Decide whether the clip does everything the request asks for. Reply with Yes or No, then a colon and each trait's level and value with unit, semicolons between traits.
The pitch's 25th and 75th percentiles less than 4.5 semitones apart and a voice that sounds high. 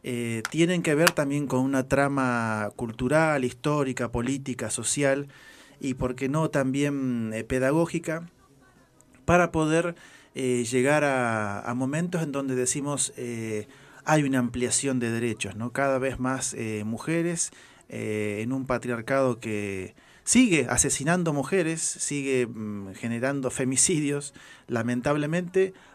No: average, 3.5 semitones; low, 130 Hz